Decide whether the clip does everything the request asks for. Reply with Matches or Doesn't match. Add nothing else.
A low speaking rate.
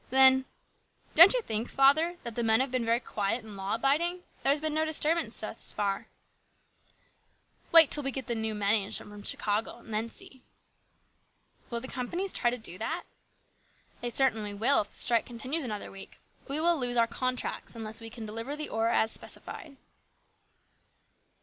Doesn't match